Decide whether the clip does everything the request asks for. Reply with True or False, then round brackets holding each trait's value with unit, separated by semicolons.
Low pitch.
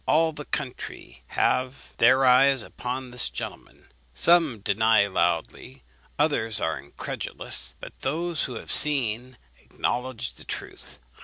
True (125 Hz)